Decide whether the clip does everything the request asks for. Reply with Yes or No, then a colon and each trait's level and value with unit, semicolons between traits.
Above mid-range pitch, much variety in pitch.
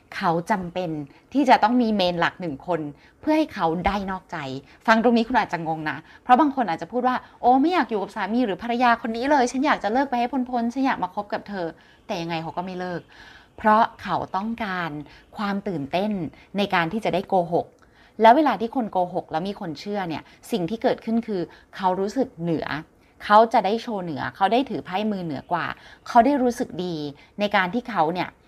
Yes: high, 200 Hz; wide, 5.7 semitones